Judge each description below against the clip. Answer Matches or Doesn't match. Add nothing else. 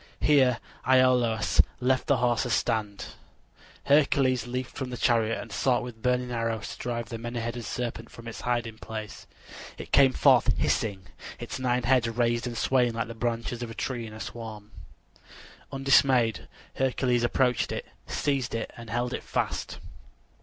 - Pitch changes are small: Matches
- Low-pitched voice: Matches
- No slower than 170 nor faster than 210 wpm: Doesn't match